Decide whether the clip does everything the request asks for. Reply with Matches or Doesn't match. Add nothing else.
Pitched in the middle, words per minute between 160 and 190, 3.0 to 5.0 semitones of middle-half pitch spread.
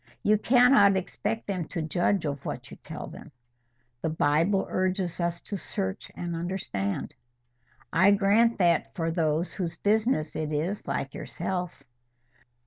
Doesn't match